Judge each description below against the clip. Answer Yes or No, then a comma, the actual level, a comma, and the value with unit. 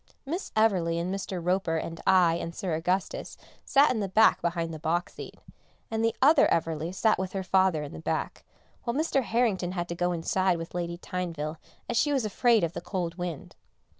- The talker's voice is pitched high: No, medium, 180 Hz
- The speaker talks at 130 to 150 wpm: No, average, 200 wpm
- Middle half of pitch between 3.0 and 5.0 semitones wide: Yes, average, 4.4 semitones